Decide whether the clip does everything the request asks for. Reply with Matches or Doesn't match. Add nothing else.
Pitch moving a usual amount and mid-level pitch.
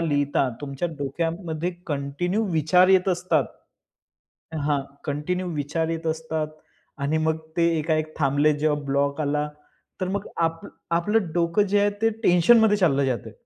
Matches